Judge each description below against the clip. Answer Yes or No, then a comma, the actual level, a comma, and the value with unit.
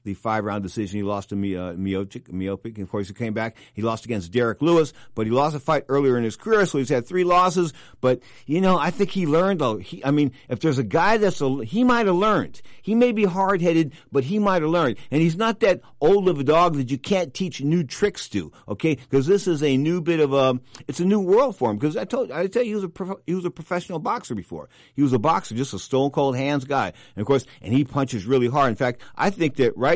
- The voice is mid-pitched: Yes, medium, 145 Hz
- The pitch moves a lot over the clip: Yes, wide, 6.3 semitones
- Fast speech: Yes, fast, 275 wpm